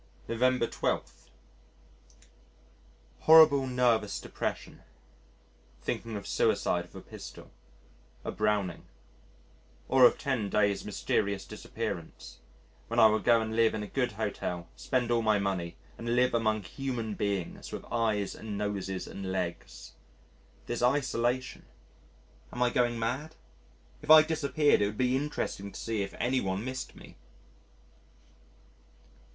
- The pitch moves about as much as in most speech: Yes, average, 3.7 semitones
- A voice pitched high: No, low, 115 Hz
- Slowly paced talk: Yes, slow, 130 wpm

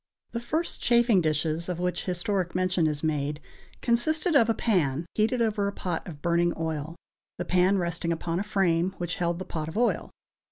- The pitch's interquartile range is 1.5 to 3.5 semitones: No, average, 4.1 semitones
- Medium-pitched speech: Yes, medium, 180 Hz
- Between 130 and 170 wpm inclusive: No, average, 190 wpm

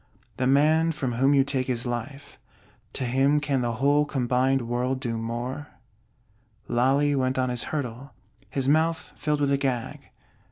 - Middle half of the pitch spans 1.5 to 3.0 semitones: Yes, narrow, 2.6 semitones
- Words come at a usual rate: Yes, average, 160 wpm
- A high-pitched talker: No, low, 135 Hz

